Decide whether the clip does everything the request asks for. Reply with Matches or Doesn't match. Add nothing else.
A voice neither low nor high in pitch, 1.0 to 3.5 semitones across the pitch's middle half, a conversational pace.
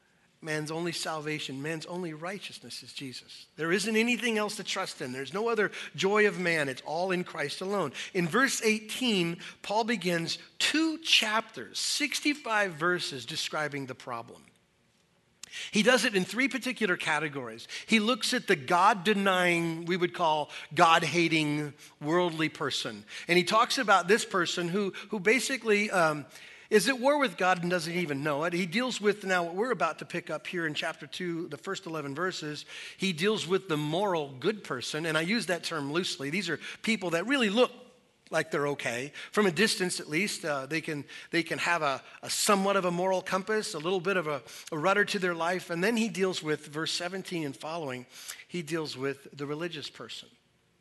Doesn't match